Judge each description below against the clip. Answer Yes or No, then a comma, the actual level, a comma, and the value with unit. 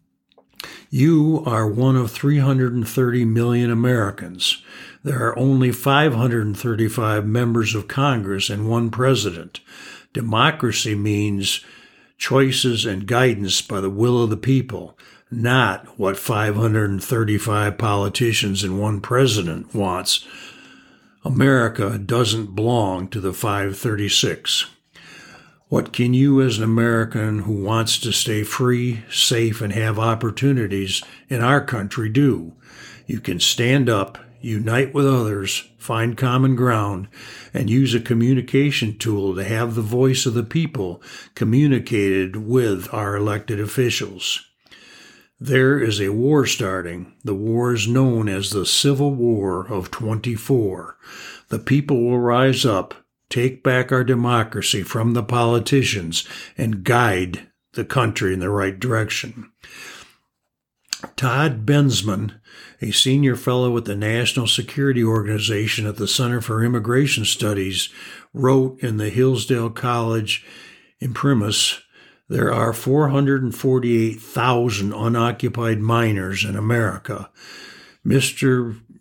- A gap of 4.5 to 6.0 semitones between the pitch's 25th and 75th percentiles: No, average, 3.3 semitones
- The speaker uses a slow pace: Yes, slow, 115 wpm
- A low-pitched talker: Yes, low, 115 Hz